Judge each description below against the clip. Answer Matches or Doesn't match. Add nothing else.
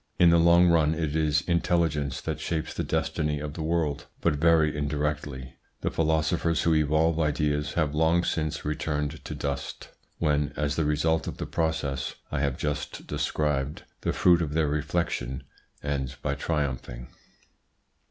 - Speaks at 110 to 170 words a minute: Matches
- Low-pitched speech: Matches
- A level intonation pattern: Matches